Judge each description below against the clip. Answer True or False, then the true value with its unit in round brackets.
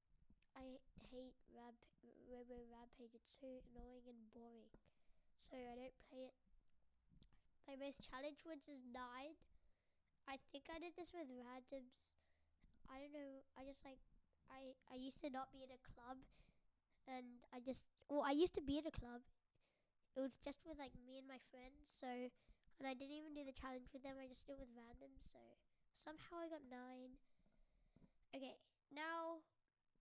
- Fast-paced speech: False (175 wpm)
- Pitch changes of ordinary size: False (2.0 semitones)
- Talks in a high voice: True (265 Hz)